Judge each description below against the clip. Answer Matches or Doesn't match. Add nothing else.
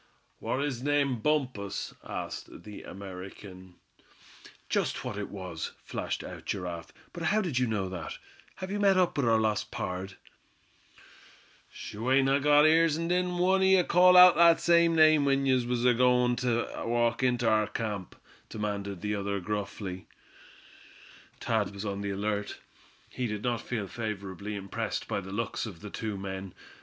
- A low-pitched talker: Matches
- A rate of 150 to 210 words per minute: Matches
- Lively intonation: Matches